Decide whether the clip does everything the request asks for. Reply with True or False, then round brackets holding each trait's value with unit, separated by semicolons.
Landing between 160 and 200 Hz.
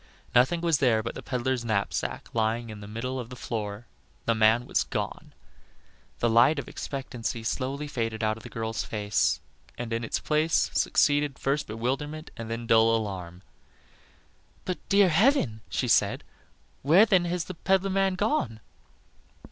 False (120 Hz)